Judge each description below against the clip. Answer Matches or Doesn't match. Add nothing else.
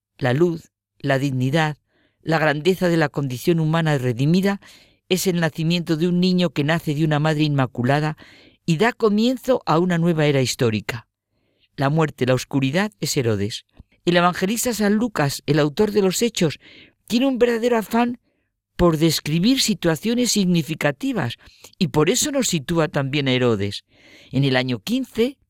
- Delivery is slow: Doesn't match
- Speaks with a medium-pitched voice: Matches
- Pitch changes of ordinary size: Doesn't match